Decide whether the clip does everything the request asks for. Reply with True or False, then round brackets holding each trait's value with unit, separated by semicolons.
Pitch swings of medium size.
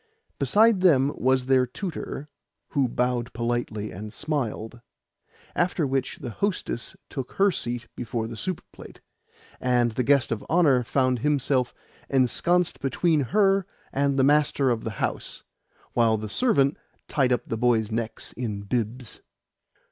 True (3.9 semitones)